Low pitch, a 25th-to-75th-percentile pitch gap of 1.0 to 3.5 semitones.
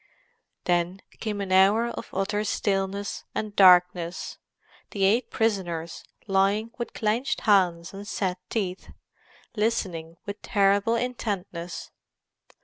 No: high, 195 Hz; average, 2.9 semitones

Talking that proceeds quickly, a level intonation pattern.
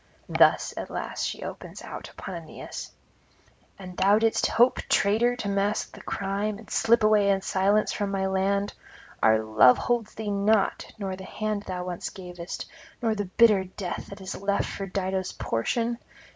No: average, 170 wpm; narrow, 2.2 semitones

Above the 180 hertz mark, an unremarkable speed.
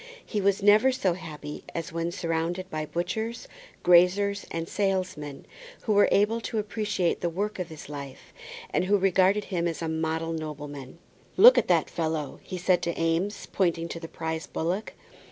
No: medium, 175 Hz; average, 170 wpm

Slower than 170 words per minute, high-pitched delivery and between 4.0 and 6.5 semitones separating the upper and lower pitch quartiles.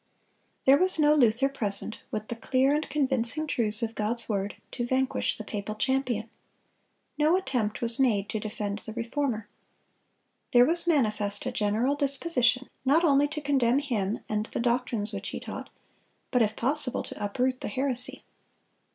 Yes: average, 160 wpm; high, 245 Hz; average, 4.3 semitones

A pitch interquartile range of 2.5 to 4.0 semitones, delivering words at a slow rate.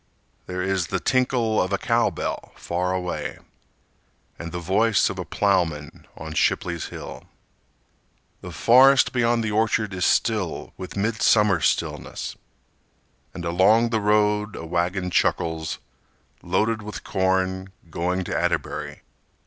Yes: average, 3.7 semitones; slow, 125 wpm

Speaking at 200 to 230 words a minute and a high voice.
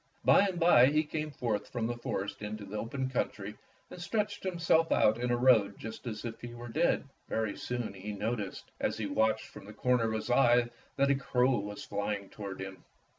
No: fast, 205 wpm; low, 120 Hz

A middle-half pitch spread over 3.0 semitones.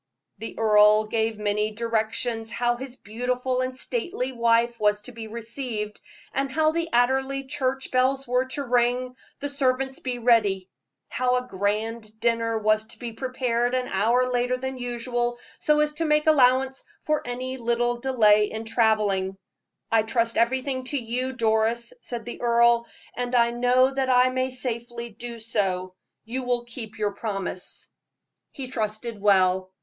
No: narrow, 2.5 semitones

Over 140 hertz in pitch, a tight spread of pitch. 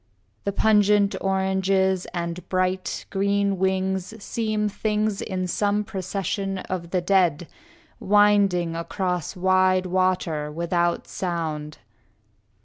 Yes: high, 190 Hz; narrow, 2.0 semitones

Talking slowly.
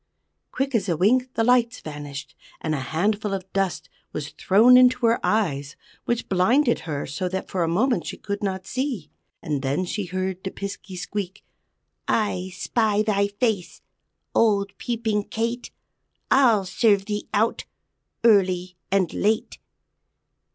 No: average, 145 wpm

